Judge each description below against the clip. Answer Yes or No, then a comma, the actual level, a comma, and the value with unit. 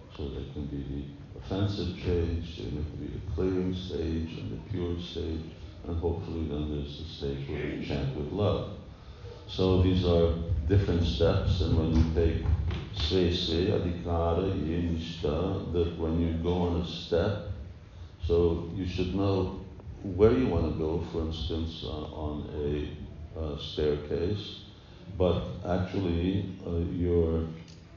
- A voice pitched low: Yes, very low, 85 Hz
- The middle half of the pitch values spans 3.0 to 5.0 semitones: No, narrow, 2.4 semitones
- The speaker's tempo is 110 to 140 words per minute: Yes, slow, 135 wpm